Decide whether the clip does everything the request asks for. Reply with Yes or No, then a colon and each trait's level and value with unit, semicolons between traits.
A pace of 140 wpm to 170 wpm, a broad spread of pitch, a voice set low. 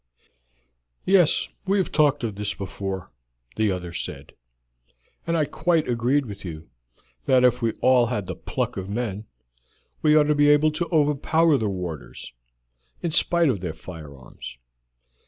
Yes: average, 155 wpm; wide, 8.0 semitones; low, 125 Hz